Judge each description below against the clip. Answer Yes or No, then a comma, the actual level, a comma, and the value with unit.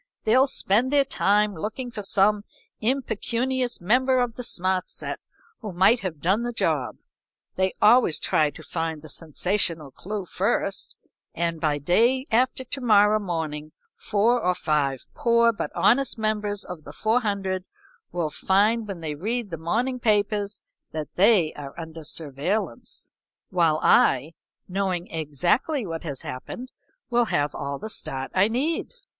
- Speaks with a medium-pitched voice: No, high, 200 Hz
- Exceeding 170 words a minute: No, average, 150 wpm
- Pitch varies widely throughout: Yes, wide, 6.2 semitones